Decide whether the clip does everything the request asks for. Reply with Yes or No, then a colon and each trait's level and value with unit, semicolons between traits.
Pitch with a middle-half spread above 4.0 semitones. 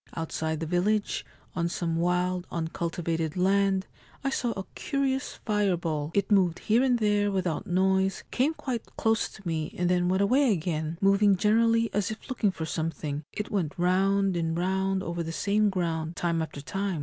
No: average, 3.7 semitones